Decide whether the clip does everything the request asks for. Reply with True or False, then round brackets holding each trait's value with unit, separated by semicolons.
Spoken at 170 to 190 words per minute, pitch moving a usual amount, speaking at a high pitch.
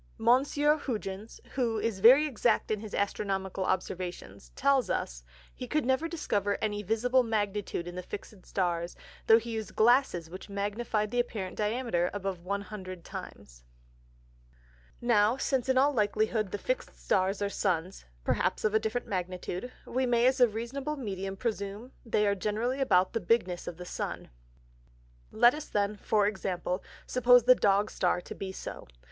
False (160 wpm; 4.1 semitones; 210 Hz)